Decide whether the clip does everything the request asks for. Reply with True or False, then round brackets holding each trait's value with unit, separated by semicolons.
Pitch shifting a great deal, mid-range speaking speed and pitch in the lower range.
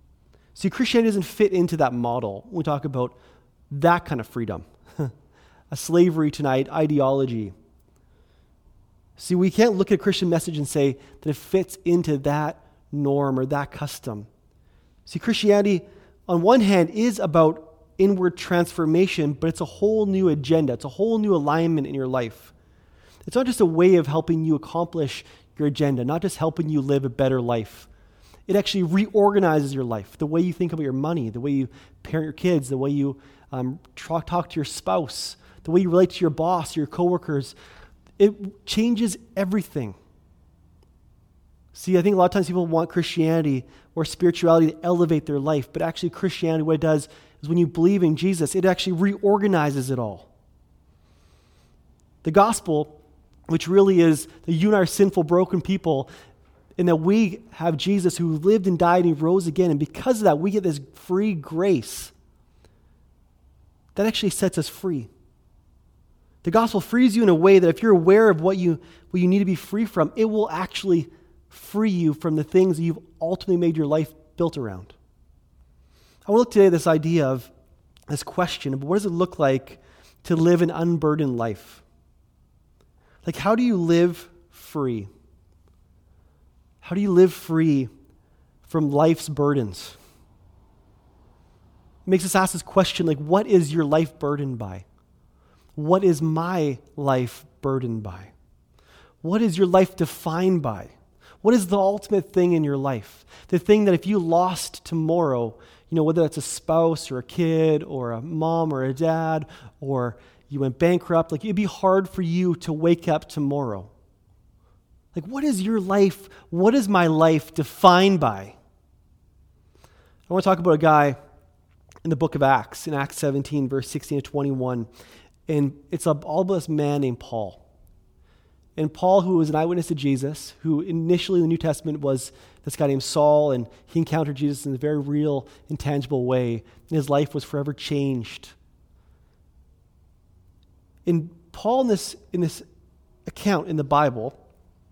False (6.8 semitones; 170 wpm; 155 Hz)